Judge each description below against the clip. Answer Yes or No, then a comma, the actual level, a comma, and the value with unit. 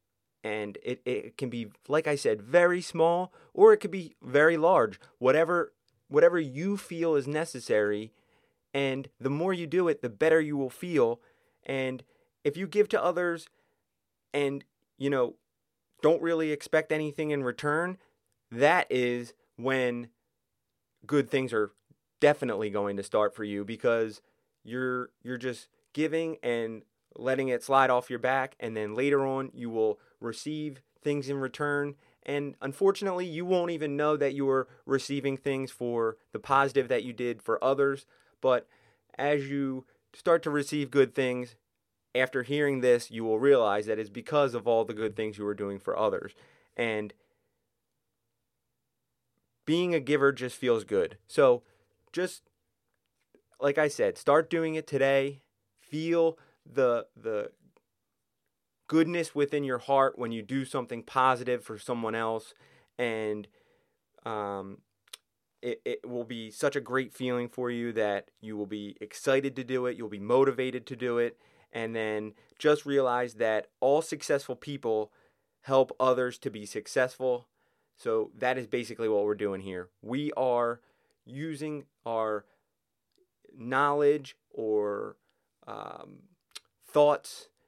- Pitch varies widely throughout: No, average, 4.2 semitones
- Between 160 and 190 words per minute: No, average, 145 wpm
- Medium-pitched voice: No, low, 130 Hz